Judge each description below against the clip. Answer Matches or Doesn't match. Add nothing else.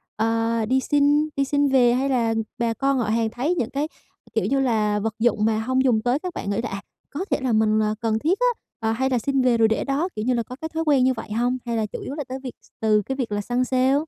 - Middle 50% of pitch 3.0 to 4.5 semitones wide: Matches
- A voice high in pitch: Matches